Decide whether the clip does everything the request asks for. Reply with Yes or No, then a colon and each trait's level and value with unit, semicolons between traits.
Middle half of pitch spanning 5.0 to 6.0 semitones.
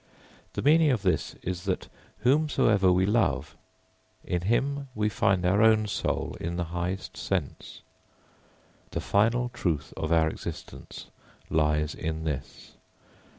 Yes: wide, 5.4 semitones